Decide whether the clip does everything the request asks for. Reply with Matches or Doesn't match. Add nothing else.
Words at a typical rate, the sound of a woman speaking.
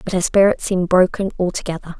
Matches